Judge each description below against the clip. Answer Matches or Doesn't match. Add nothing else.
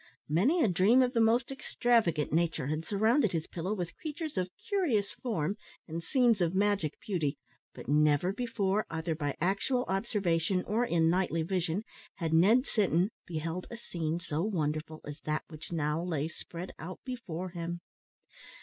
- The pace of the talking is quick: Doesn't match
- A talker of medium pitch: Matches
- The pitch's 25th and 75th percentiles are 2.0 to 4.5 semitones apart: Doesn't match